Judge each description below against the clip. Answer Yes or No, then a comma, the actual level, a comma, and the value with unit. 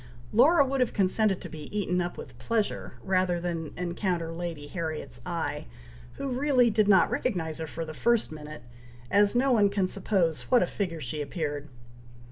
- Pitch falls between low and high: Yes, medium, 180 Hz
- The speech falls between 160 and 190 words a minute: Yes, average, 175 wpm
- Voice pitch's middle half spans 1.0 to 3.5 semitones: No, average, 5.2 semitones